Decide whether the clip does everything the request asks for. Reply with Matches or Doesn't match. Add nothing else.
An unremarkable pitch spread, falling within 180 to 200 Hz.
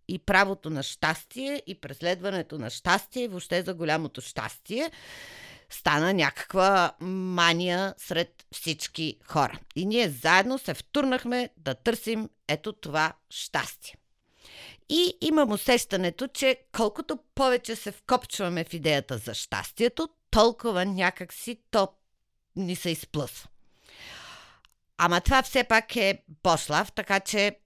Doesn't match